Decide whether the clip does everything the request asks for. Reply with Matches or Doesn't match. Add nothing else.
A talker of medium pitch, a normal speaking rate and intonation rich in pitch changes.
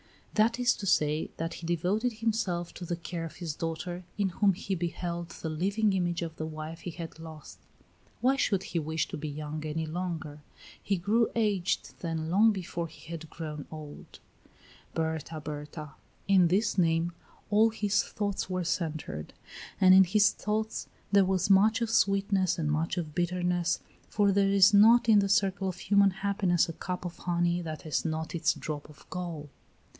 Doesn't match